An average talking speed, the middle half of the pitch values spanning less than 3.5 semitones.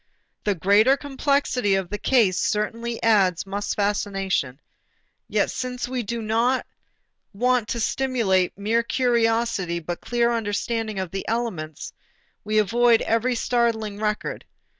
No: slow, 125 wpm; average, 3.1 semitones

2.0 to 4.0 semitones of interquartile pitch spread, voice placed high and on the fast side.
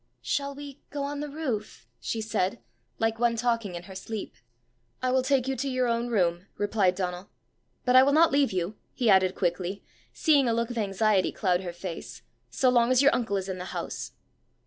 No: wide, 5.4 semitones; high, 225 Hz; fast, 215 wpm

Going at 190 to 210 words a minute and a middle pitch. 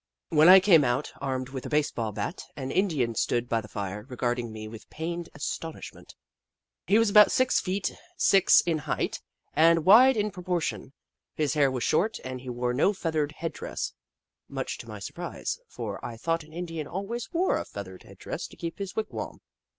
Yes: average, 195 wpm; medium, 160 Hz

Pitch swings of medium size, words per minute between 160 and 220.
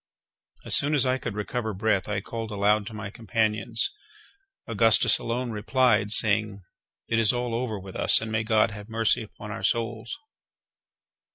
No: narrow, 1.8 semitones; average, 165 wpm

